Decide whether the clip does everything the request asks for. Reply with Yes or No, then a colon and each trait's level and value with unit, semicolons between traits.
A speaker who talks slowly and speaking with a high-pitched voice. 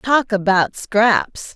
Yes: slow, 115 wpm; high, 215 Hz